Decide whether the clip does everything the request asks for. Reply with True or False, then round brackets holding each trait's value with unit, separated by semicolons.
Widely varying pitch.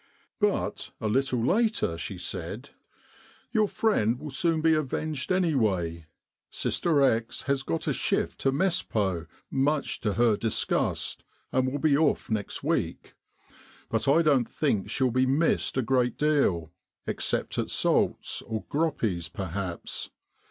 True (6.4 semitones)